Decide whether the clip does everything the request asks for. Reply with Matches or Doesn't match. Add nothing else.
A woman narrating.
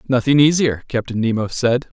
Doesn't match